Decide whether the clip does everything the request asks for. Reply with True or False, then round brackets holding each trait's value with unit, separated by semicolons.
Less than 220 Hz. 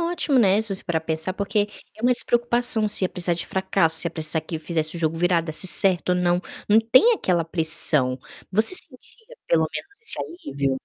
True (185 Hz)